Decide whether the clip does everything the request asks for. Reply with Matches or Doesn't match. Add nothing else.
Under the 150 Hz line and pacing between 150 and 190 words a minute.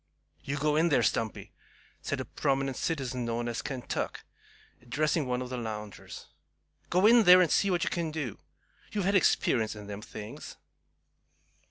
Matches